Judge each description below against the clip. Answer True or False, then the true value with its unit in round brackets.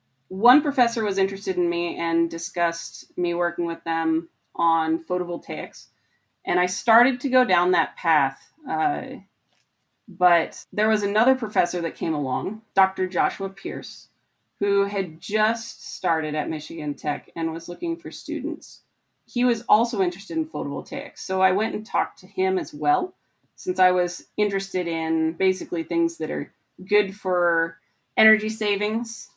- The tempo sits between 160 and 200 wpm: False (150 wpm)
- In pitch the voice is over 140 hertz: True (185 Hz)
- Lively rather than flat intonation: False (4.3 semitones)